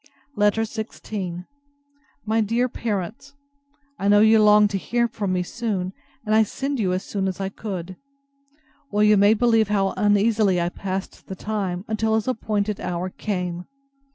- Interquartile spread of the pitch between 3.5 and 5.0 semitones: No, average, 2.7 semitones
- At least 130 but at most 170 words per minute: Yes, average, 160 wpm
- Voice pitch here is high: Yes, high, 205 Hz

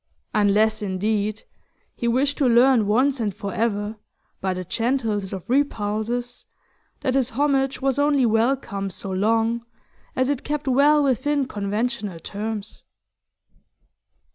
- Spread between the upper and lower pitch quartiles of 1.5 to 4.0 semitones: No, average, 4.5 semitones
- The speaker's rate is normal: No, slow, 125 wpm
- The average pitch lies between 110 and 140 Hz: No, high, 230 Hz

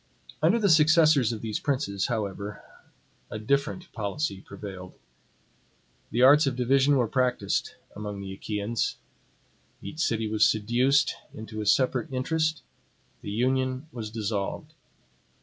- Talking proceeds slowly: Yes, slow, 125 wpm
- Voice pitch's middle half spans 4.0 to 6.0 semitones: Yes, average, 4.8 semitones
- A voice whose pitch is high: No, low, 120 Hz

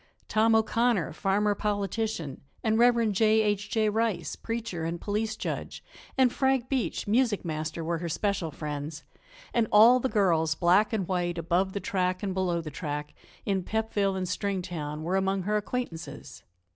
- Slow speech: No, average, 160 wpm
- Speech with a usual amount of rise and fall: Yes, average, 4.4 semitones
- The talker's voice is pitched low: No, high, 195 Hz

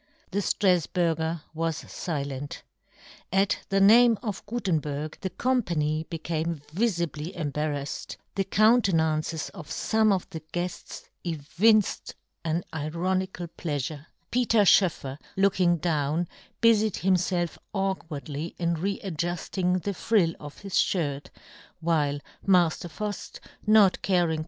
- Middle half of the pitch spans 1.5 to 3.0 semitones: No, average, 3.8 semitones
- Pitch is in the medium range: Yes, medium, 175 Hz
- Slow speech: Yes, slow, 120 wpm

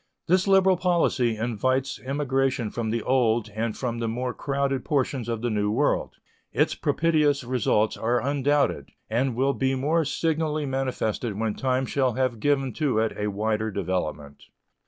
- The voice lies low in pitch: Yes, low, 130 Hz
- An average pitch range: Yes, average, 3.8 semitones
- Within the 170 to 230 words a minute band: No, average, 155 wpm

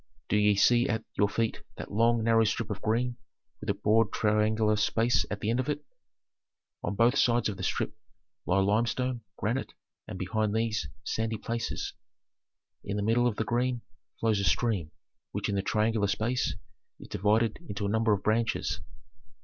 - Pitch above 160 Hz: No, low, 110 Hz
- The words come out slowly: No, average, 175 wpm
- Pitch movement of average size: No, narrow, 2.1 semitones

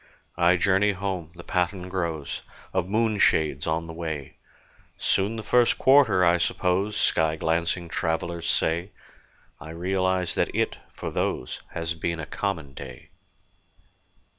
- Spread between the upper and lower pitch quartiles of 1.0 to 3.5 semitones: Yes, average, 2.8 semitones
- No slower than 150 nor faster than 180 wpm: No, slow, 135 wpm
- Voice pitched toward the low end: Yes, very low, 85 Hz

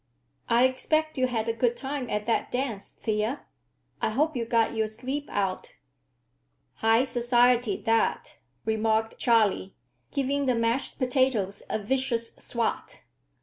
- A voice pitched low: No, high, 235 Hz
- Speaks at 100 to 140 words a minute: Yes, slow, 135 wpm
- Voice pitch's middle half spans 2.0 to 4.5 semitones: Yes, average, 2.8 semitones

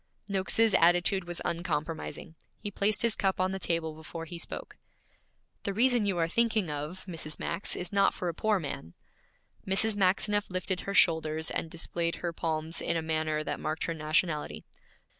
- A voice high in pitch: No, medium, 175 Hz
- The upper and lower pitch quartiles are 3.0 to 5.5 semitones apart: Yes, average, 3.5 semitones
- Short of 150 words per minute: No, average, 175 wpm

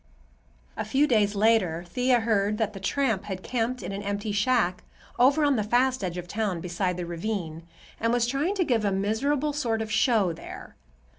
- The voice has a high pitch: Yes, high, 220 Hz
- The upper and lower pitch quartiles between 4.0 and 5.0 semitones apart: Yes, average, 4.3 semitones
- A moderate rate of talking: Yes, average, 195 wpm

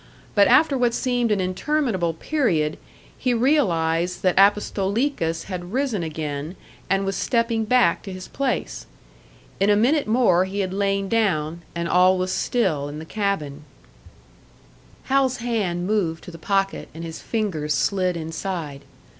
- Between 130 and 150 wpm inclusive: Yes, average, 145 wpm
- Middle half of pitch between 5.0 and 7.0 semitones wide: Yes, wide, 5.5 semitones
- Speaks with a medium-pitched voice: No, high, 195 Hz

